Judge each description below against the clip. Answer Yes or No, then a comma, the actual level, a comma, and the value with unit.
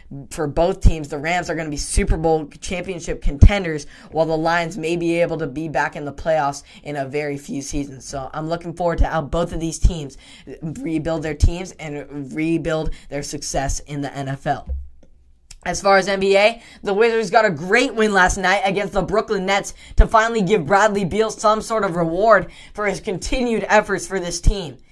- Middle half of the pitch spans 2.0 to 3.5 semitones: No, average, 4.9 semitones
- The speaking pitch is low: No, medium, 170 Hz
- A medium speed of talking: Yes, average, 195 wpm